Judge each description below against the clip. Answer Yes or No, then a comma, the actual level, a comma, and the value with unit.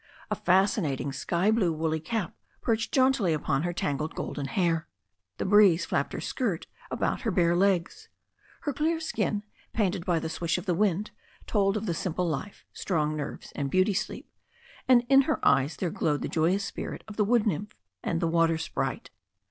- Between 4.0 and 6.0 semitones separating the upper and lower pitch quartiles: Yes, average, 4.7 semitones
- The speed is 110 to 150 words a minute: No, average, 180 wpm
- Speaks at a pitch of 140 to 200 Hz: Yes, medium, 185 Hz